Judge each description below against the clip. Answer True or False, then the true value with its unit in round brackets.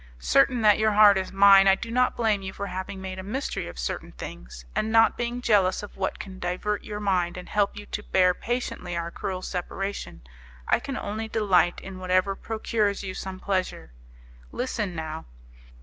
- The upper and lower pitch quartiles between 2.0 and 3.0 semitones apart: True (2.6 semitones)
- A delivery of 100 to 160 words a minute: False (190 wpm)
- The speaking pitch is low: False (195 Hz)